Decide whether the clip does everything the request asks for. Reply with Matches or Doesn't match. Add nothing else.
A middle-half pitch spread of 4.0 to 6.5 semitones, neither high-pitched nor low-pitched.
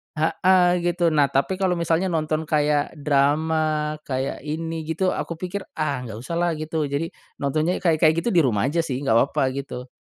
Doesn't match